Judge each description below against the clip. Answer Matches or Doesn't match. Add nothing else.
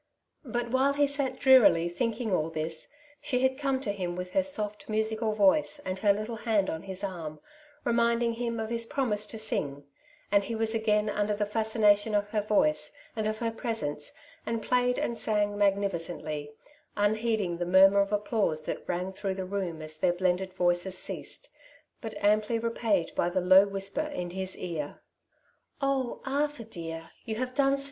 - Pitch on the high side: Matches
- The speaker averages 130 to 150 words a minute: Doesn't match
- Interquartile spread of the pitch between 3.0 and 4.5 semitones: Matches